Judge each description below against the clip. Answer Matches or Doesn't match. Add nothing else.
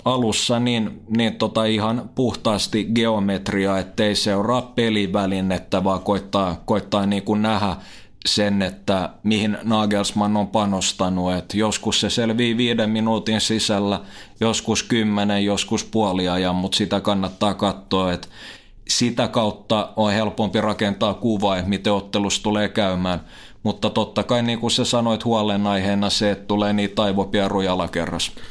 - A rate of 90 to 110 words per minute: Doesn't match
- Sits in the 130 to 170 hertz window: Doesn't match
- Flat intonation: Matches